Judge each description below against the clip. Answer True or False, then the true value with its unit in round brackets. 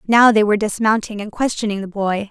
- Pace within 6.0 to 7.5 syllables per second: True (6.1 syllables/s)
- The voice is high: True (210 Hz)